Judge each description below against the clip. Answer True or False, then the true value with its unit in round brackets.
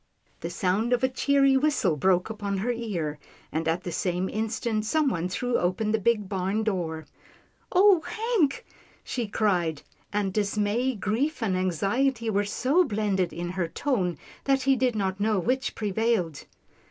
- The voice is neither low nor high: False (210 Hz)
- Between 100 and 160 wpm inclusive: True (155 wpm)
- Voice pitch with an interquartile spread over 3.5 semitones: True (5.2 semitones)